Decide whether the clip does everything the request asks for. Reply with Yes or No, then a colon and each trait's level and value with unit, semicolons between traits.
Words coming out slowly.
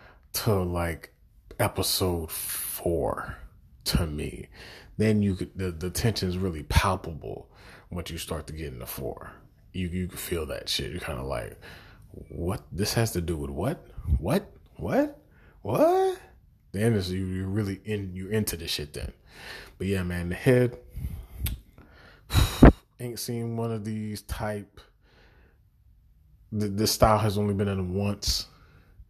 No: average, 150 wpm